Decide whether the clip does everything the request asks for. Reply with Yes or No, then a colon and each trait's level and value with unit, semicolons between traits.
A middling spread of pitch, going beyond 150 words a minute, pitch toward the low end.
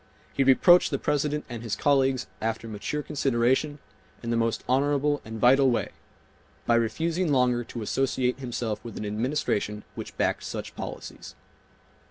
No: average, 3.7 semitones; average, 145 wpm; low, 125 Hz